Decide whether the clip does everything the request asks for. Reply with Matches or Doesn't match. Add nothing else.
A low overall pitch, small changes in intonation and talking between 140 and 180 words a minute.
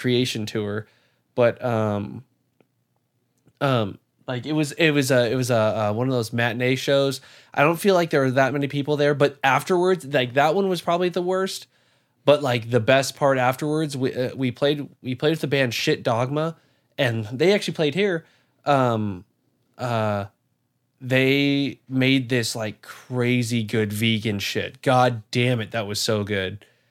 Doesn't match